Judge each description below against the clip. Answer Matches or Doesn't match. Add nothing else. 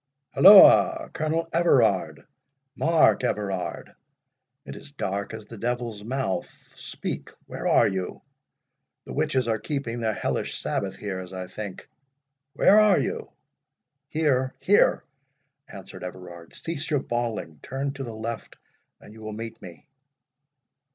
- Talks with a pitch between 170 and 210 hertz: Doesn't match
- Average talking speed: Doesn't match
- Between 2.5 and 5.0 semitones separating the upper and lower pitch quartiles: Doesn't match